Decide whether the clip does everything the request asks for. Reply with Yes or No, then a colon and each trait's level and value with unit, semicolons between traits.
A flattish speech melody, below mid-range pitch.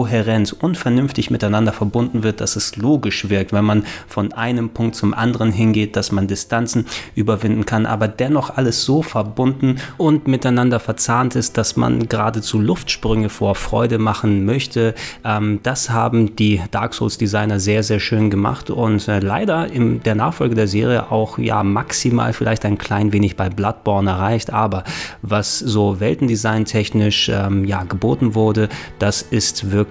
Yes: narrow, 2.1 semitones; low, 110 Hz